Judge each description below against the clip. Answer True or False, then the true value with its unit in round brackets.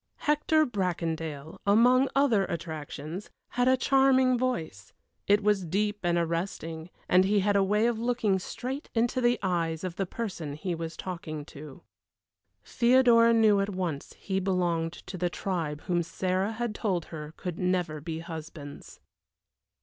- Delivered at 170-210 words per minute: False (150 wpm)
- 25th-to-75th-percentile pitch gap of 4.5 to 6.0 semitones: True (5.6 semitones)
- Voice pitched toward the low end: False (185 Hz)